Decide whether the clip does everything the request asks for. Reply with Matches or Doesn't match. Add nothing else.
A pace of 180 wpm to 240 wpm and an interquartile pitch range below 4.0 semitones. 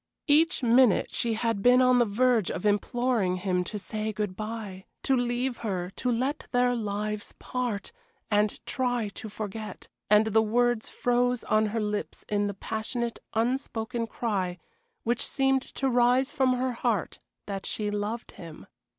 Doesn't match